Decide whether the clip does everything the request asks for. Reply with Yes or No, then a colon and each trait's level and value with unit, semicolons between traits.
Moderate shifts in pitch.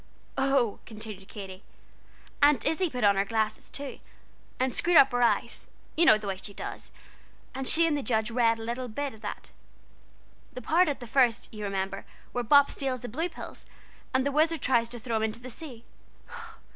Yes: average, 4.1 semitones